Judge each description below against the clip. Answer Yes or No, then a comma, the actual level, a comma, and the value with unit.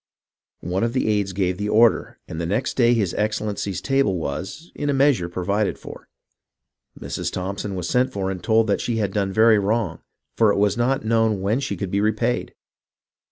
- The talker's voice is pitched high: No, low, 105 Hz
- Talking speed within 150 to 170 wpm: No, average, 195 wpm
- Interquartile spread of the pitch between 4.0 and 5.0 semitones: No, average, 3.3 semitones